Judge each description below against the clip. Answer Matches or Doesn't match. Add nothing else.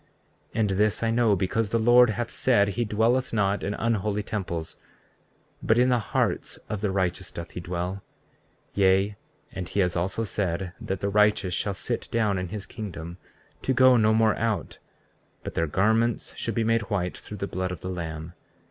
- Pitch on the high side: Doesn't match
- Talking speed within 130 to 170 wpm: Doesn't match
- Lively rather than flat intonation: Doesn't match